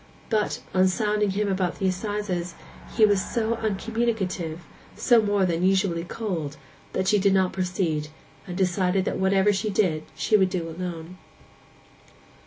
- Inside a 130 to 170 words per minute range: Yes, average, 150 wpm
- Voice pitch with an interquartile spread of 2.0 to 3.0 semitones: Yes, narrow, 2.6 semitones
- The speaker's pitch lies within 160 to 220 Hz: Yes, high, 190 Hz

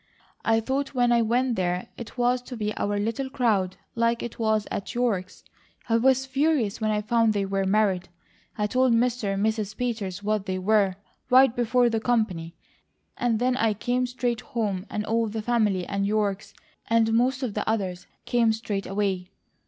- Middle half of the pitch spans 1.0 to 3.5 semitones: Yes, average, 3.2 semitones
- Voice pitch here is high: Yes, high, 220 Hz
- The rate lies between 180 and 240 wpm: Yes, average, 185 wpm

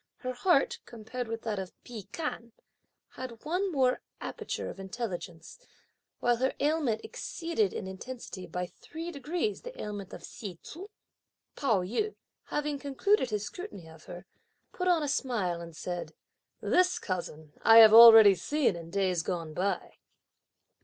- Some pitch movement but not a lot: No, wide, 7.9 semitones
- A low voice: No, high, 230 Hz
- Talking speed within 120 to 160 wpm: Yes, average, 150 wpm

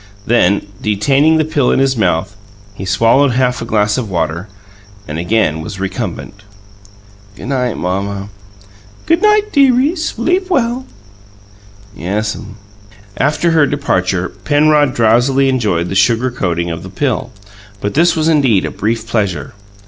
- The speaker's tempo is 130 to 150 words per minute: Yes, average, 140 wpm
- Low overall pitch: Yes, low, 115 Hz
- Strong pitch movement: Yes, wide, 7.0 semitones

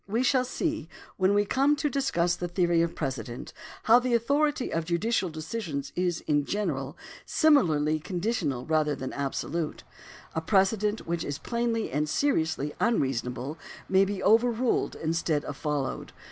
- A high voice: No, medium, 175 Hz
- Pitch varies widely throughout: Yes, wide, 7.3 semitones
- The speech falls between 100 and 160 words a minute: Yes, average, 145 wpm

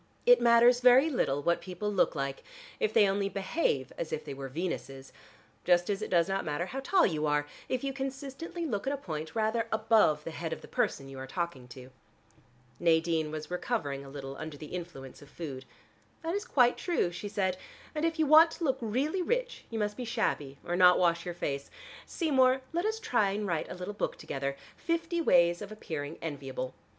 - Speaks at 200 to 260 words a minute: Yes, fast, 205 wpm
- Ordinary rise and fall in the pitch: No, wide, 9.0 semitones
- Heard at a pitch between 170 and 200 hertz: Yes, medium, 185 Hz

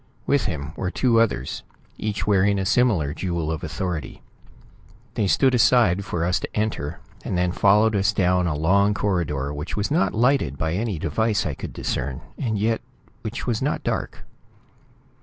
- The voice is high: No, low, 100 Hz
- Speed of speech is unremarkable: Yes, average, 170 wpm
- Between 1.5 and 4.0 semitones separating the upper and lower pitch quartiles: No, average, 4.8 semitones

